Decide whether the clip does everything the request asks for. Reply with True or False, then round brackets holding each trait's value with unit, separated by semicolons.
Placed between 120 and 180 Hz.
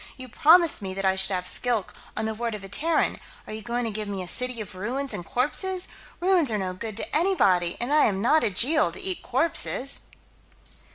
False (235 Hz)